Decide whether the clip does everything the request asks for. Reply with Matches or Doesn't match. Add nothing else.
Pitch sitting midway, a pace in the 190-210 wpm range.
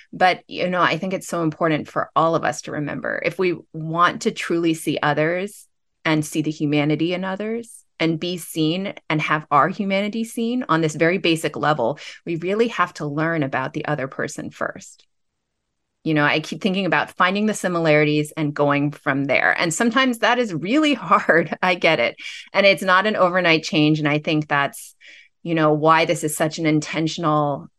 Matches